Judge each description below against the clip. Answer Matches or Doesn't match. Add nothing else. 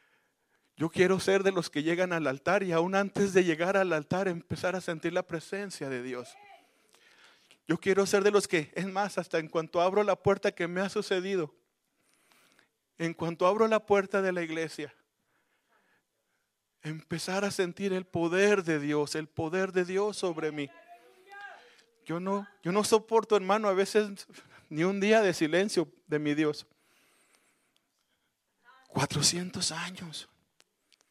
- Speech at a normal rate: Matches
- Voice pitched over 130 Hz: Matches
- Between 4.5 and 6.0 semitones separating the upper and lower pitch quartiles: Doesn't match